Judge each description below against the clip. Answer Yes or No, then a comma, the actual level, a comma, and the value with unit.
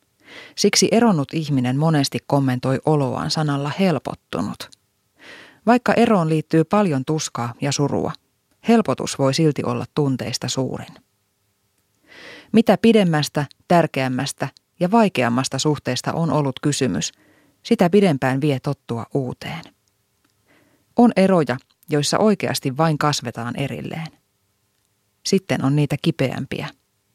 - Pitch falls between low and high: Yes, medium, 145 Hz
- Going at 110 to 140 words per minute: No, average, 100 wpm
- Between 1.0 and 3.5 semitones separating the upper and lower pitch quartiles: No, average, 4.4 semitones